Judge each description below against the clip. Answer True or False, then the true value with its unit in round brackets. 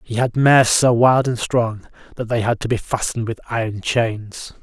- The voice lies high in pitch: False (115 Hz)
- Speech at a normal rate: False (210 wpm)